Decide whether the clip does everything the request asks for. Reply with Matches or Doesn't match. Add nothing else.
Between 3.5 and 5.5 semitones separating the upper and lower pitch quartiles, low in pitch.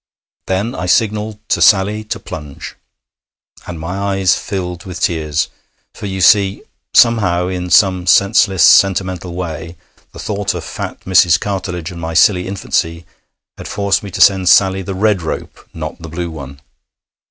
Doesn't match